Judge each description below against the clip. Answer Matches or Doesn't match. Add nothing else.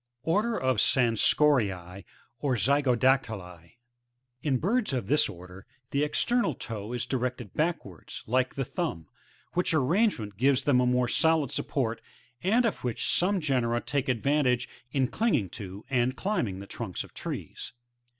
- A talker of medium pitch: Doesn't match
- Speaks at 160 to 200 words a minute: Doesn't match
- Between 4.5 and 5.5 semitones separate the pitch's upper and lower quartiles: Matches